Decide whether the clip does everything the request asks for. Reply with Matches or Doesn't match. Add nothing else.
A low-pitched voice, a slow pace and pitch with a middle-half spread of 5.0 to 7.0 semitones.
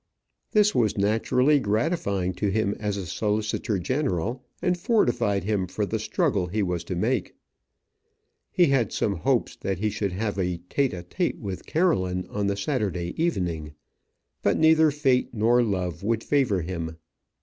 Doesn't match